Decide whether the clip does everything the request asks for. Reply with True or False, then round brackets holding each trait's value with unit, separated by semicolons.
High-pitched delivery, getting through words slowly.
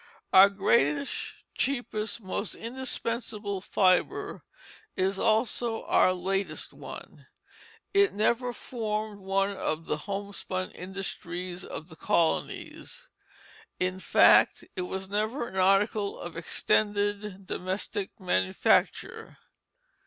True (195 Hz; 100 wpm)